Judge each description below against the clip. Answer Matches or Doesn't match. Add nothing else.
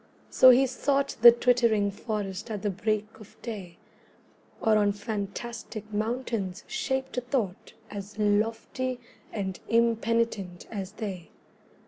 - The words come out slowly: Matches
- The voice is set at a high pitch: Matches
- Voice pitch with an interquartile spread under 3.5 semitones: Matches